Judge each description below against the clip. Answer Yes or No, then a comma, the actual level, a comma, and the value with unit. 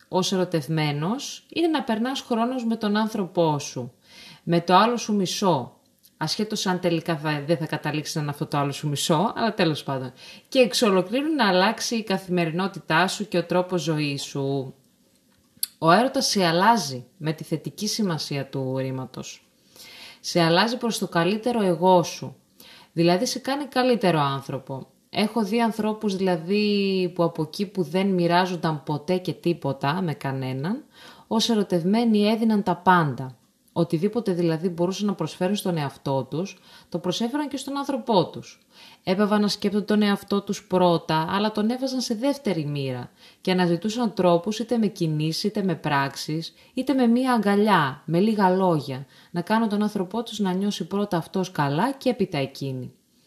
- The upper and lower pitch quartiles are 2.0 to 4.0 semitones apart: No, average, 5.2 semitones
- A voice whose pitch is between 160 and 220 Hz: Yes, medium, 185 Hz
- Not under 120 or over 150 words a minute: No, average, 160 wpm